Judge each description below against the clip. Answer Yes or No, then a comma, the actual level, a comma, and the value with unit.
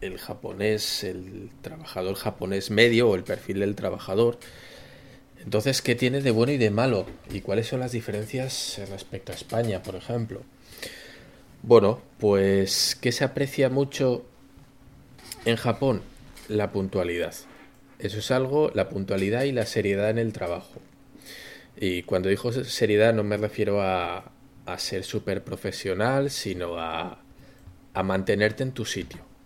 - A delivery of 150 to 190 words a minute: No, average, 140 wpm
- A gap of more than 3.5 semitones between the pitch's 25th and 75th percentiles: Yes, average, 4.7 semitones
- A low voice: Yes, low, 110 Hz